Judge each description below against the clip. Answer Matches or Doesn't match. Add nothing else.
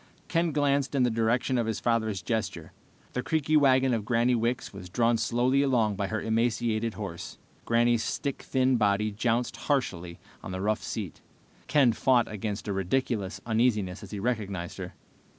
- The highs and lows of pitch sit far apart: Doesn't match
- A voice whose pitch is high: Doesn't match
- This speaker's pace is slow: Doesn't match